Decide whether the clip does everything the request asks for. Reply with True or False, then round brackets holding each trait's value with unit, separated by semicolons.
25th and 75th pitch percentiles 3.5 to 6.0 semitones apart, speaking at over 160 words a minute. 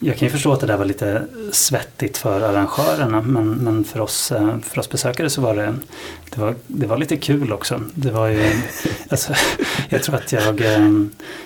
True (4.5 semitones; 195 wpm)